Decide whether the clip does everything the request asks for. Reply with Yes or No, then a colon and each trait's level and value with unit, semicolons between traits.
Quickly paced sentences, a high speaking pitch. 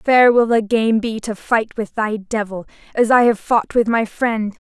Yes: fast, 220 wpm; high, 225 Hz